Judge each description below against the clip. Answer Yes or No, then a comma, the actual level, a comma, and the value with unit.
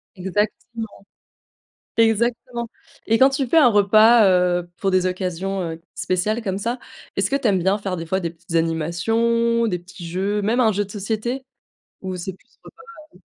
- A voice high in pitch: Yes, high, 200 Hz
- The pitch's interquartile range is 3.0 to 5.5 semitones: Yes, average, 4.2 semitones